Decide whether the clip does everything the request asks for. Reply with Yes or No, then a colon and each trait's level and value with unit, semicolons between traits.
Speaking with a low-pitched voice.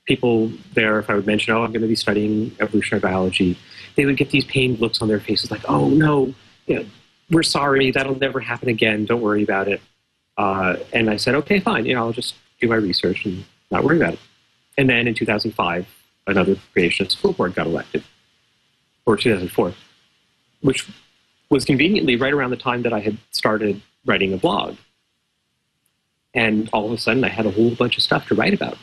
Yes: low, 115 Hz